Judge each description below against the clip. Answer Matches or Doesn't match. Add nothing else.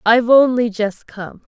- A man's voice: Doesn't match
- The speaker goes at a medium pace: Matches